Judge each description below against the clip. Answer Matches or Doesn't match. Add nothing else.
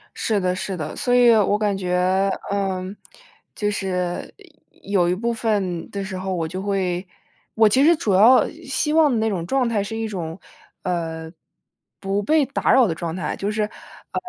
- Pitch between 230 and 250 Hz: Doesn't match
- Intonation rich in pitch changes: Doesn't match